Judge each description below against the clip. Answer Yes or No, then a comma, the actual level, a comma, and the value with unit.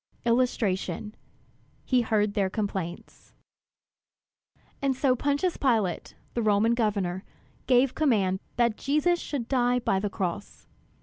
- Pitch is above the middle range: Yes, high, 230 Hz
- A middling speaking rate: No, slow, 115 wpm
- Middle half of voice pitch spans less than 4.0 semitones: No, average, 4.3 semitones